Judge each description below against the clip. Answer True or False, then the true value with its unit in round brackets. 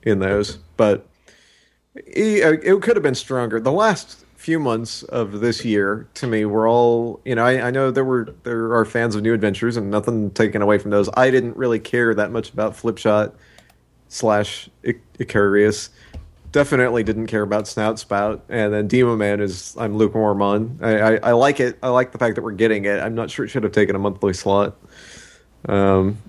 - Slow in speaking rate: False (205 wpm)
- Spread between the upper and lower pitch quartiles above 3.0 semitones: False (2.5 semitones)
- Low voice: True (110 Hz)